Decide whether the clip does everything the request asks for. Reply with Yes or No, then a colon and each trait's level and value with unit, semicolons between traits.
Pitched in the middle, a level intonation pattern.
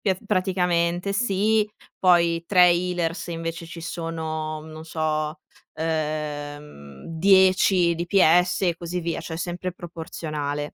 Yes: medium, 170 Hz; narrow, 2.3 semitones